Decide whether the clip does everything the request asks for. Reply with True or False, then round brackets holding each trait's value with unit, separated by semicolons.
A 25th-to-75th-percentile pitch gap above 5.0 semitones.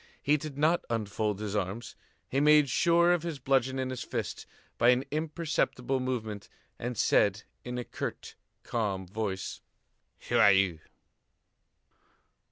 True (5.6 semitones)